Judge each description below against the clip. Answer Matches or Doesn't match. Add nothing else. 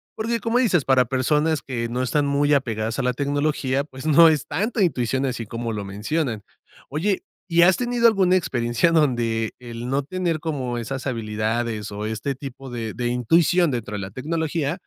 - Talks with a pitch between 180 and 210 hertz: Doesn't match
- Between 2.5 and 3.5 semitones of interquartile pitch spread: Doesn't match